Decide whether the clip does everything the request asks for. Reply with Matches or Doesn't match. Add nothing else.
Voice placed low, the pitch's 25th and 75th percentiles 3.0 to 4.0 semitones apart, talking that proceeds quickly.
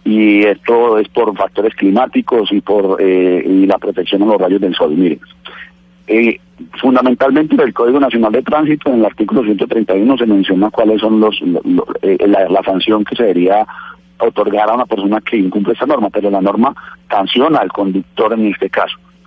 Matches